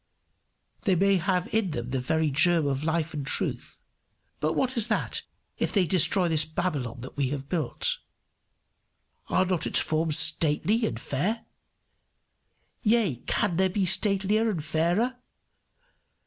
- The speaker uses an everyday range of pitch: Yes, average, 4.8 semitones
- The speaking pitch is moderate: Yes, medium, 175 Hz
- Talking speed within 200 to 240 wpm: No, average, 145 wpm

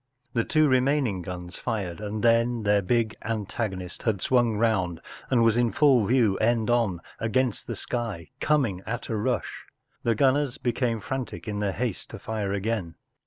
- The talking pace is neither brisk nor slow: Yes, average, 165 wpm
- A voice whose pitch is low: Yes, low, 115 Hz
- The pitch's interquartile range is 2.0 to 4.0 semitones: Yes, average, 3.2 semitones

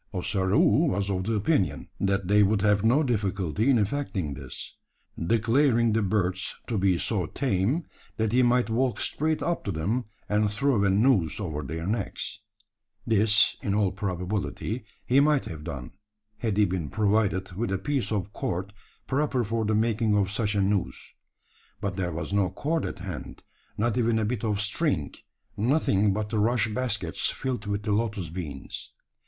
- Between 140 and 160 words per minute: No, average, 170 wpm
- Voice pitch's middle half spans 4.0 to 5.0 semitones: No, average, 3.4 semitones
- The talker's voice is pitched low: Yes, low, 105 Hz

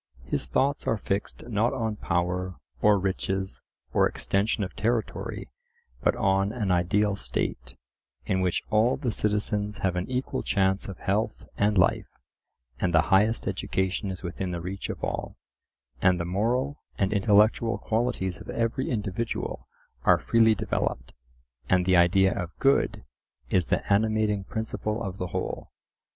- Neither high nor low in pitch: No, low, 100 Hz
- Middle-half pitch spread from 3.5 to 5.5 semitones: No, average, 2.9 semitones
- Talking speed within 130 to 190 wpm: Yes, average, 150 wpm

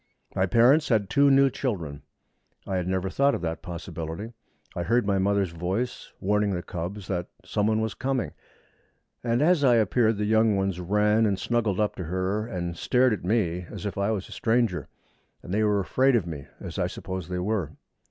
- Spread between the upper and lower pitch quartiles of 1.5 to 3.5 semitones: No, average, 4.2 semitones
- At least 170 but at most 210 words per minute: Yes, average, 195 wpm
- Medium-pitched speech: No, low, 100 Hz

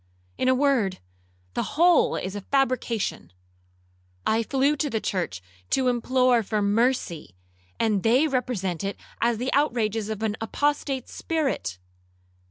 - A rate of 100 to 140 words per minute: Yes, slow, 135 wpm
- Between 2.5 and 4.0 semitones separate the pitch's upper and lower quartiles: No, average, 4.5 semitones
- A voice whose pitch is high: Yes, high, 235 Hz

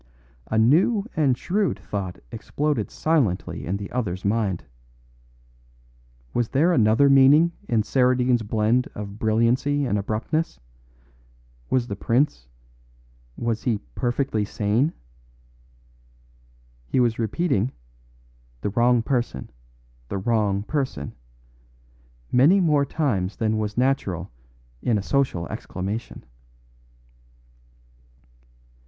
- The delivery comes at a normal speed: No, slow, 100 wpm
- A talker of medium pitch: No, low, 120 Hz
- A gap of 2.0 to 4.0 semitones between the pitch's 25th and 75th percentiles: No, average, 4.9 semitones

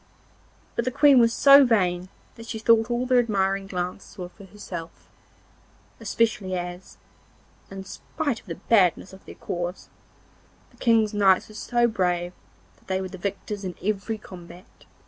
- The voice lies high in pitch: Yes, high, 195 Hz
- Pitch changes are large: No, average, 3.9 semitones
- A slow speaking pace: No, average, 160 wpm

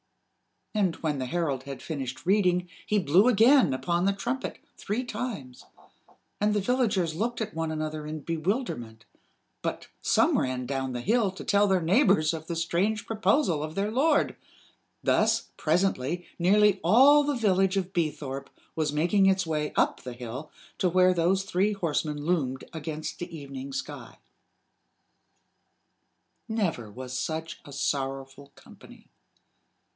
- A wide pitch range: Yes, wide, 5.8 semitones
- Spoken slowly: No, average, 145 wpm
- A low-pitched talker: No, medium, 170 Hz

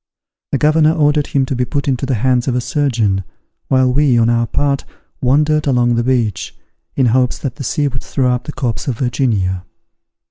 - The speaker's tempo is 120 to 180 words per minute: No, average, 200 wpm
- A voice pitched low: Yes, low, 130 Hz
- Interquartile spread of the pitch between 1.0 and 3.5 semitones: Yes, average, 2.8 semitones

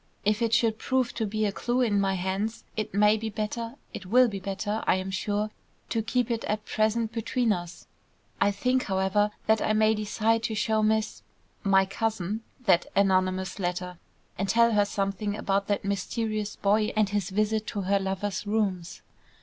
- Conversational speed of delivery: Yes, average, 185 wpm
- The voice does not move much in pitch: Yes, narrow, 2.2 semitones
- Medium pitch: No, high, 210 Hz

